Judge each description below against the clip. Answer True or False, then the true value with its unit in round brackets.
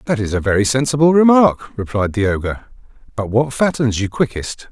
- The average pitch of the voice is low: True (120 Hz)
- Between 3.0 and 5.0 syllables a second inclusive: False (5.6 syllables/s)